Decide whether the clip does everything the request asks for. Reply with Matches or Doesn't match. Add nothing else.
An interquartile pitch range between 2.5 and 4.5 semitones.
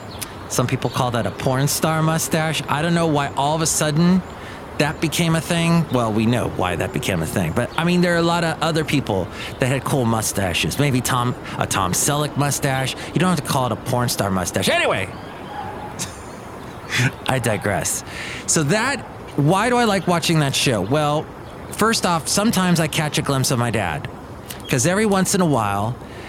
Doesn't match